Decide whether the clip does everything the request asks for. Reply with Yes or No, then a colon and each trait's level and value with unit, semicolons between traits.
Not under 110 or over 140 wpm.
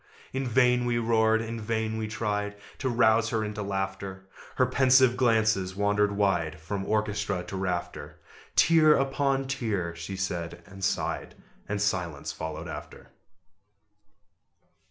Yes: slow, 135 wpm